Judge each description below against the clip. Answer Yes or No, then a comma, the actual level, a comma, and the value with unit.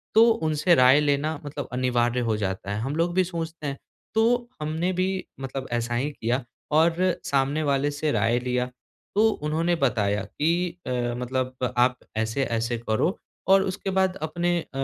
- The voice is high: No, medium, 145 Hz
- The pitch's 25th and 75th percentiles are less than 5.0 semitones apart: No, wide, 5.4 semitones